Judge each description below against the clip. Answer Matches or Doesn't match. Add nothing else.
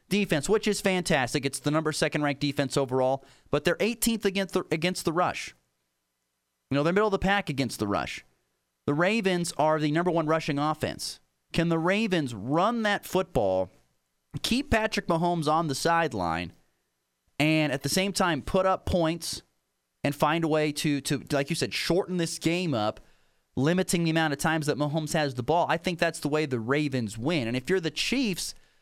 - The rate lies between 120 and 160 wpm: Doesn't match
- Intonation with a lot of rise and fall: Doesn't match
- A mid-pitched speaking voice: Matches